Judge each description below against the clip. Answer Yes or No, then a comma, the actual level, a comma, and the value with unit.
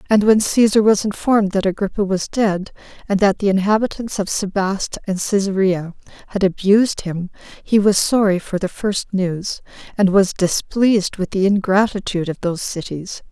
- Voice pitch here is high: Yes, high, 195 Hz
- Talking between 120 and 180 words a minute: Yes, average, 160 wpm